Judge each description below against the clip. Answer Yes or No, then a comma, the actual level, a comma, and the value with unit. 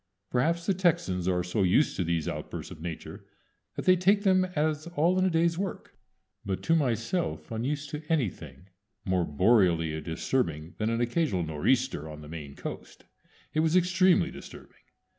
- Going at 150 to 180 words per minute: Yes, average, 165 wpm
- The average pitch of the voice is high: No, low, 120 Hz